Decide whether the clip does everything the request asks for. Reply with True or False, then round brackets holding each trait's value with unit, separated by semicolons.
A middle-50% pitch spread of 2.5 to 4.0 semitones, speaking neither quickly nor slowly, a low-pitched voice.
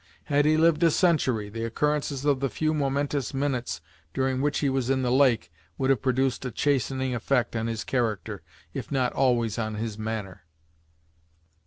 True (3.6 semitones; 175 wpm; 130 Hz)